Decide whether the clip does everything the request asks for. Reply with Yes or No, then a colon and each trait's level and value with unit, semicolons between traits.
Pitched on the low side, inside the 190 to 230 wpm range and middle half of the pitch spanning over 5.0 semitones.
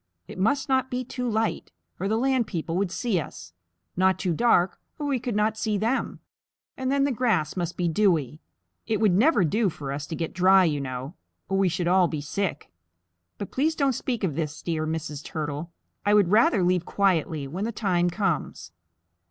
No: high, 190 Hz; average, 200 wpm; wide, 5.6 semitones